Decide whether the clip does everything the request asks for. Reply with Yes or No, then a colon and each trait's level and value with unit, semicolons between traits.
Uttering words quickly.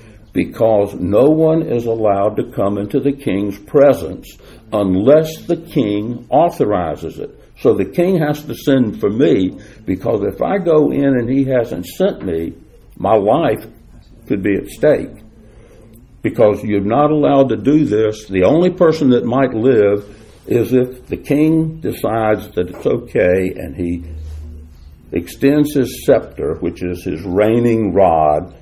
No: average, 150 wpm